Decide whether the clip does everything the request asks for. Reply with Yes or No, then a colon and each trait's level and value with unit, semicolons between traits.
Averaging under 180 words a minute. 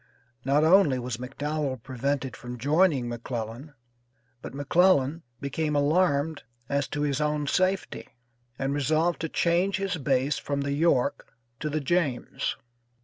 Yes: slow, 135 wpm